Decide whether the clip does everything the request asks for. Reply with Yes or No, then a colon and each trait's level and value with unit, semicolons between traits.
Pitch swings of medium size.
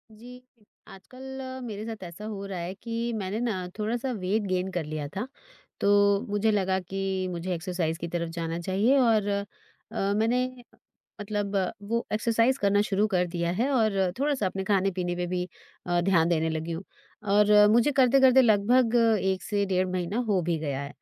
Yes: average, 3.9 semitones